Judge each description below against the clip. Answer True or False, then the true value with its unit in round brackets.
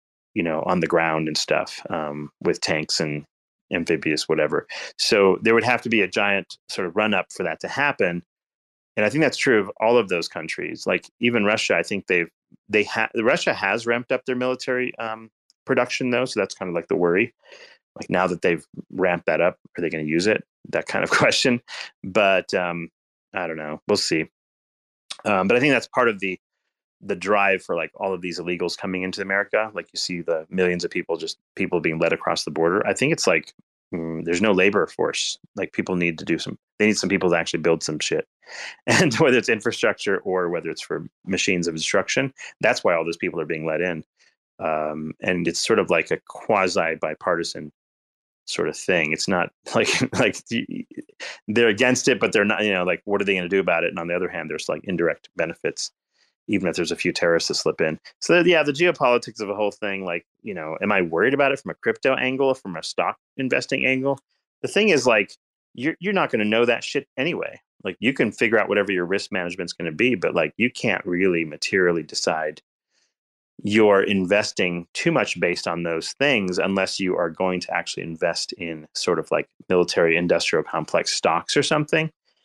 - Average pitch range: False (6.1 semitones)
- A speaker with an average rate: False (220 wpm)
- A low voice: True (95 Hz)